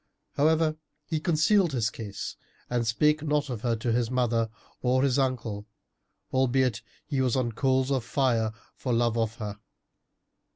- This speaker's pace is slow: No, average, 155 wpm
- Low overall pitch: Yes, low, 125 Hz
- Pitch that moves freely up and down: No, average, 3.4 semitones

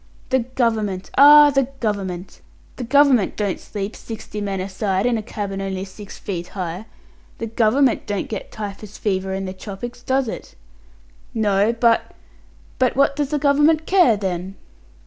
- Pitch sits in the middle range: No, high, 215 Hz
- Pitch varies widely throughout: No, average, 4.8 semitones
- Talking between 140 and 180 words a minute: Yes, average, 165 wpm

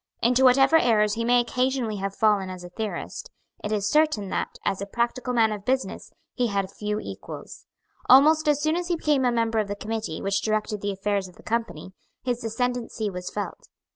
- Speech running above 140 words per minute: Yes, average, 200 wpm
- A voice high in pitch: Yes, high, 225 Hz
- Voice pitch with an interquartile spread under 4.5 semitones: Yes, average, 3.7 semitones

